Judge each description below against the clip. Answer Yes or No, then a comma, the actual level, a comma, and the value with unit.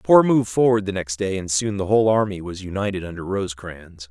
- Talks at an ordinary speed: No, fast, 235 wpm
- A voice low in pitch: Yes, low, 100 Hz